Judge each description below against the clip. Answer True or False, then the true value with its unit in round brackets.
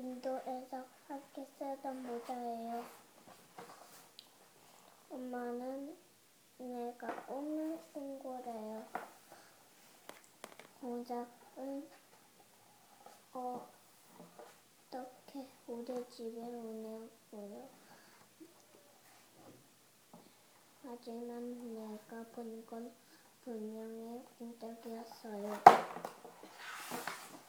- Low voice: False (245 Hz)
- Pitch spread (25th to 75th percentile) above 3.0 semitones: False (2.2 semitones)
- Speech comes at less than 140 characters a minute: True (115 characters per minute)